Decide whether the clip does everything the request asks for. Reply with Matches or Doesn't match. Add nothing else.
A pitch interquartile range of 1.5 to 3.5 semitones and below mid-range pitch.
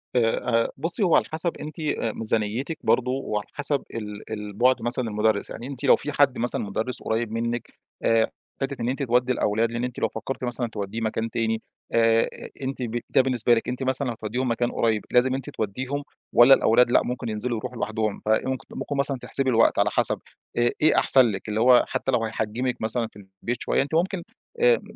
Matches